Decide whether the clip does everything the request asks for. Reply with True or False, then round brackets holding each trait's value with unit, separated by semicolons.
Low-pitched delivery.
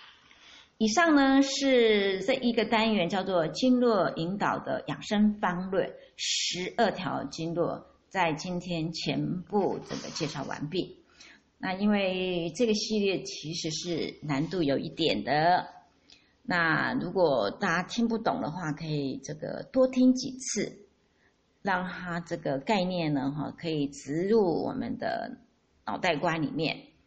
False (185 Hz)